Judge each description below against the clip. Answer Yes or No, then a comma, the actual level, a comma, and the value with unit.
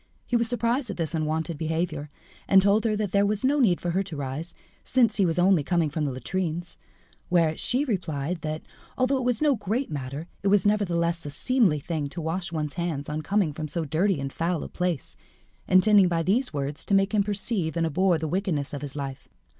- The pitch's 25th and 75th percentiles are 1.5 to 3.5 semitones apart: No, average, 4.6 semitones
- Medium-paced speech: No, fast, 215 wpm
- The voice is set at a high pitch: No, medium, 175 Hz